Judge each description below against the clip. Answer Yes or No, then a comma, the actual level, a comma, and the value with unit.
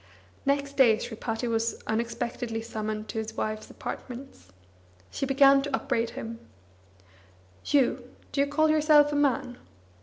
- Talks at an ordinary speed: No, slow, 130 wpm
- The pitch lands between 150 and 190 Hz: No, high, 245 Hz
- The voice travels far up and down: No, average, 3.8 semitones